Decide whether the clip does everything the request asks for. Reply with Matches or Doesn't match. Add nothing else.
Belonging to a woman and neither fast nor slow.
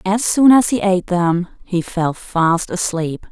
Matches